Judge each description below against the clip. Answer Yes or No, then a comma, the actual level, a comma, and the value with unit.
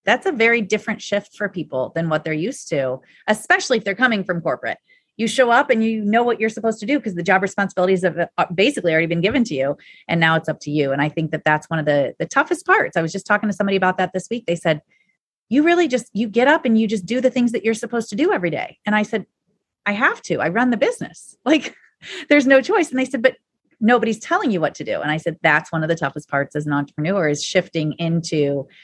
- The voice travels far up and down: Yes, wide, 6.9 semitones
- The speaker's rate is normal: No, fast, 265 wpm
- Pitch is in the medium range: No, high, 205 Hz